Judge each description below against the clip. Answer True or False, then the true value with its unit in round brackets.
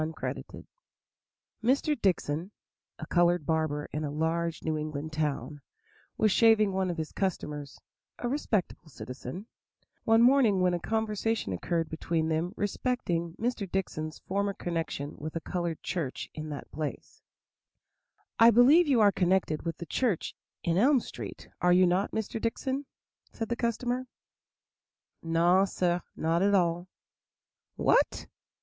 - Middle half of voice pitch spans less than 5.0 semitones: False (5.5 semitones)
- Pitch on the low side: False (175 Hz)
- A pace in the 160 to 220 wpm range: False (145 wpm)